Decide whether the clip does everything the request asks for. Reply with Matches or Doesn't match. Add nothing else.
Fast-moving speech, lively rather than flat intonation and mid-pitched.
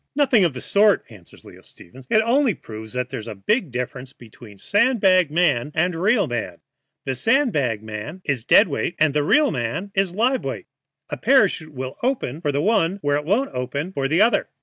Matches